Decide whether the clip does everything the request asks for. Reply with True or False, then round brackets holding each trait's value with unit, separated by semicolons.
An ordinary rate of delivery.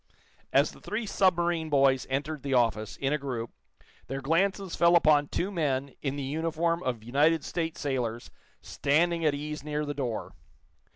True (165 wpm)